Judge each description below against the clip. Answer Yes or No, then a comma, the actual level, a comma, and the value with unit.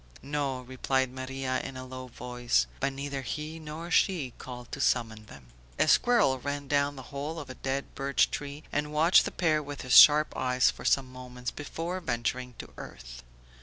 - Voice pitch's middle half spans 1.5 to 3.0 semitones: Yes, narrow, 2.6 semitones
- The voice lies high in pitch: No, low, 135 Hz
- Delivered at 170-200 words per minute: Yes, average, 185 wpm